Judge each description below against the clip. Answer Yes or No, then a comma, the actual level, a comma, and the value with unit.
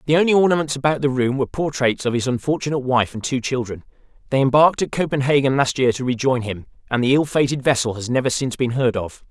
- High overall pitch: No, low, 135 Hz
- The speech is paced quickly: Yes, fast, 225 wpm